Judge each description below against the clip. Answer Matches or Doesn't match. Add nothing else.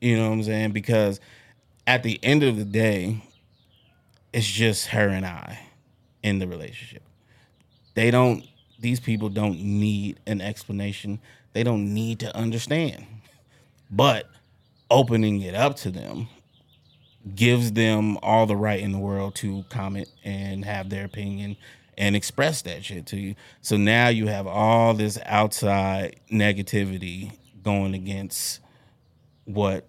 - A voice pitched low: Matches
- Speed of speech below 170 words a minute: Matches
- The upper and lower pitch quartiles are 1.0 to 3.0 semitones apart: Matches